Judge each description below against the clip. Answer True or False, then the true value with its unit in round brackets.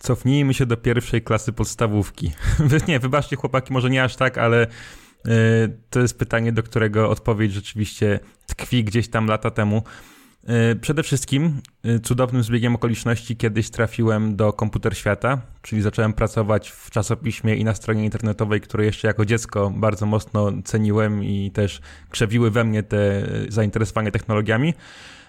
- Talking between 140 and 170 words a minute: True (155 wpm)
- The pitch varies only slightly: True (2.0 semitones)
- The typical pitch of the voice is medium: False (115 Hz)